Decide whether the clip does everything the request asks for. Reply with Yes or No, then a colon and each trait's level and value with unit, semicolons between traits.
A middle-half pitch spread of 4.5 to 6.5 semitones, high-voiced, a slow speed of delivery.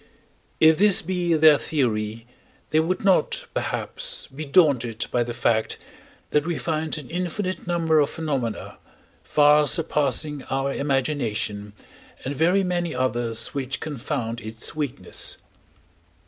No: average, 5.1 semitones; medium, 150 Hz; slow, 125 wpm